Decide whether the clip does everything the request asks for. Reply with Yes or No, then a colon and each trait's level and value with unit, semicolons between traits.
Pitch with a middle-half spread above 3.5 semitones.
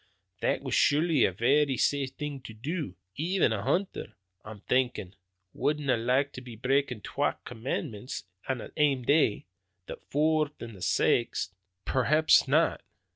Yes: average, 4.4 semitones